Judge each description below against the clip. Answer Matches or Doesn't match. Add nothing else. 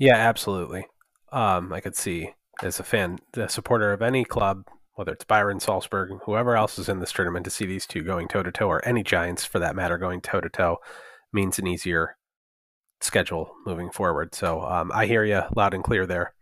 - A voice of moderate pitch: Doesn't match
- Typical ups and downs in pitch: Matches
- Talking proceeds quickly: Matches